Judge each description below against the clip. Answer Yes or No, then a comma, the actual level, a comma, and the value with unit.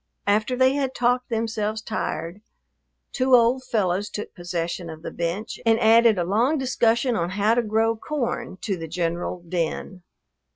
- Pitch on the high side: Yes, high, 220 Hz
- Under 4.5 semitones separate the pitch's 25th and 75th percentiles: No, average, 5.0 semitones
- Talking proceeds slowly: No, average, 160 wpm